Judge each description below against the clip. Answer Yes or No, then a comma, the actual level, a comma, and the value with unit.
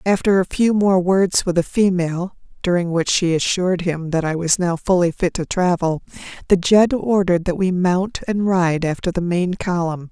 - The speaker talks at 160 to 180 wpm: No, average, 195 wpm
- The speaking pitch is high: No, medium, 180 Hz